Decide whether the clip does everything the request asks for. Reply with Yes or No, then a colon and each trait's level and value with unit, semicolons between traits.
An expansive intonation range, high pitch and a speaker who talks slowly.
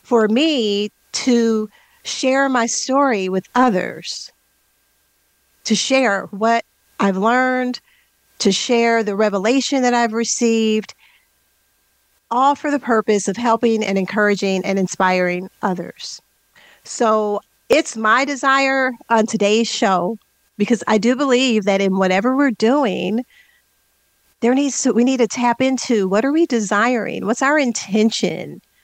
No: average, 3.5 semitones; high, 230 Hz; slow, 130 wpm